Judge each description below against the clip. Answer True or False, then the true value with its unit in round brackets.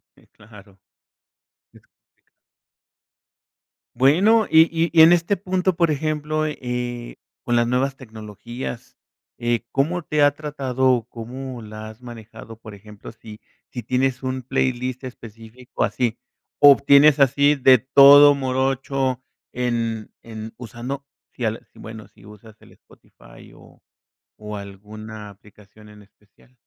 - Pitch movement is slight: False (3.9 semitones)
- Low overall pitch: True (125 Hz)